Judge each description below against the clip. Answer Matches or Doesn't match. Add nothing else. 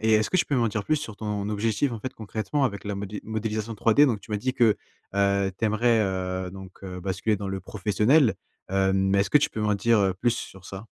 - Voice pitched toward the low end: Matches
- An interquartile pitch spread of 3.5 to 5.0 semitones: Doesn't match